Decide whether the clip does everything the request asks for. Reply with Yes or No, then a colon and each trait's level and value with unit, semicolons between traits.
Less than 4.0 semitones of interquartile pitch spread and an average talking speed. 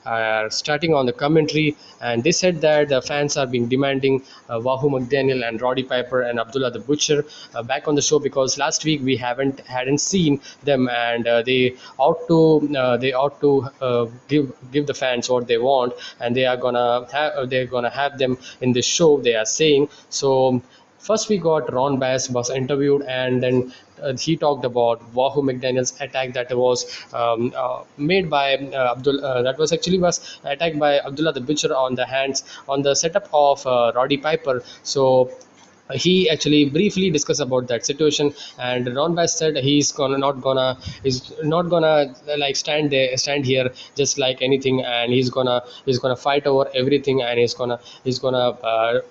Yes: average, 2.7 semitones; average, 190 wpm